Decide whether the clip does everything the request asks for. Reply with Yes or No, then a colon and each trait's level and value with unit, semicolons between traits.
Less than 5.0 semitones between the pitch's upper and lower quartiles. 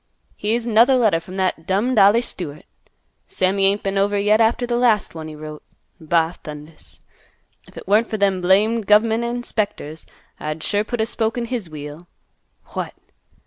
No: average, 5.3 semitones